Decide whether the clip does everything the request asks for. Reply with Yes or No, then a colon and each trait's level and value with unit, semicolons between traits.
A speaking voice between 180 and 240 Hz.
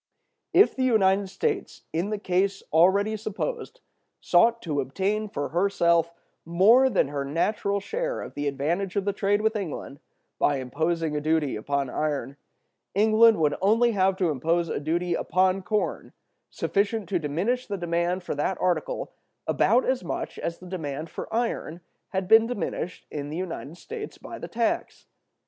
Yes: medium, 185 Hz